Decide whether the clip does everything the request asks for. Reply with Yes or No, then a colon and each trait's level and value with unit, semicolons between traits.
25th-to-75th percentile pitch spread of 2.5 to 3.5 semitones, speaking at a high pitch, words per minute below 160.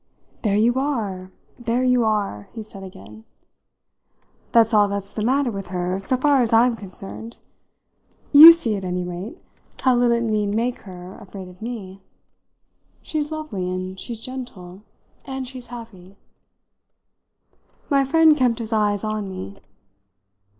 No: average, 4.6 semitones; high, 220 Hz; average, 145 wpm